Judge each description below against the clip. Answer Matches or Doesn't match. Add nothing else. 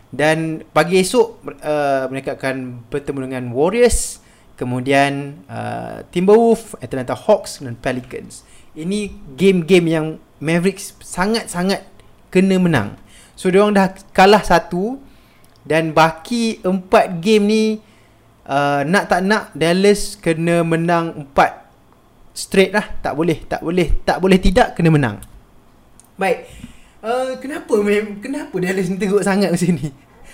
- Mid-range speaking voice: Matches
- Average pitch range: Doesn't match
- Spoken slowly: Doesn't match